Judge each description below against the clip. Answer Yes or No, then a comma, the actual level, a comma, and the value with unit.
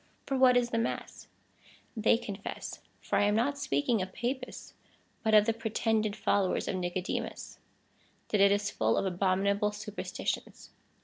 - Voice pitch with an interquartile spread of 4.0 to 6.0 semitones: No, average, 2.7 semitones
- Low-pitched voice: No, high, 210 Hz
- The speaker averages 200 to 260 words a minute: No, average, 160 wpm